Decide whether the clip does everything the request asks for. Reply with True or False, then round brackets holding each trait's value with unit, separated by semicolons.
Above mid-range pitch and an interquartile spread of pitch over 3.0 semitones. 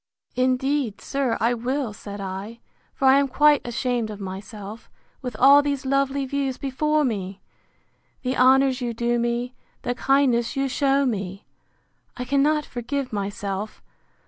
True (250 Hz; 3.5 semitones)